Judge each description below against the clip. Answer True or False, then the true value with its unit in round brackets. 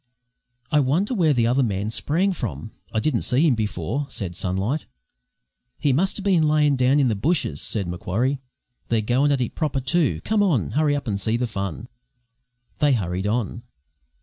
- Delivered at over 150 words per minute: True (175 wpm)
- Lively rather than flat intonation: True (5.9 semitones)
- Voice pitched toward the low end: True (130 Hz)